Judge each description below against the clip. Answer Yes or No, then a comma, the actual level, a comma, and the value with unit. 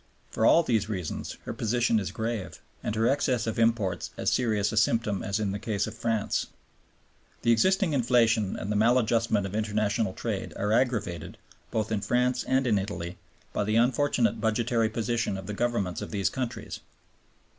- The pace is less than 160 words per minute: No, average, 175 wpm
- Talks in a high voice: No, low, 110 Hz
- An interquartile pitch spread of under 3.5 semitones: Yes, narrow, 2.5 semitones